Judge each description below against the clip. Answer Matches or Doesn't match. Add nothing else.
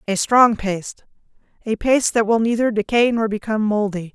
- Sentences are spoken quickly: Doesn't match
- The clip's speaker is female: Matches